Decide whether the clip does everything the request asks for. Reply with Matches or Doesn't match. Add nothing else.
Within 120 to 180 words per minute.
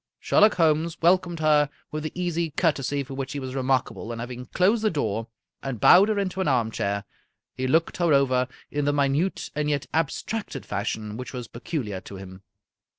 Doesn't match